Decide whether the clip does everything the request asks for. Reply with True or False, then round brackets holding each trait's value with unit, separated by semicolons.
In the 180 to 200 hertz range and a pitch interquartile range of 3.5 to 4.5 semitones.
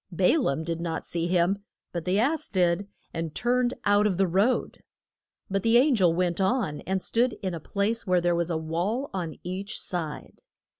True (185 Hz; 3.8 semitones)